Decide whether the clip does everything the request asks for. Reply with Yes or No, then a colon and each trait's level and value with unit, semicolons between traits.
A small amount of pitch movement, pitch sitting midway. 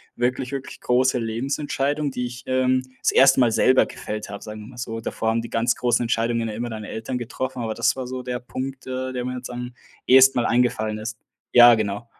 No: narrow, 2.2 semitones; low, 125 Hz